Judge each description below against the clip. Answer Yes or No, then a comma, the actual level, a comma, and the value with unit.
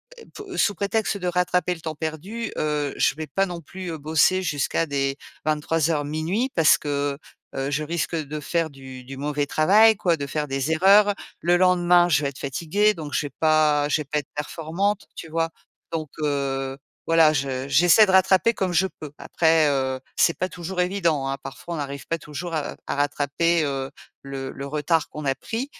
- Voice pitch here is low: No, medium, 155 Hz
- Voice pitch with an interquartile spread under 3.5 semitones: No, average, 3.8 semitones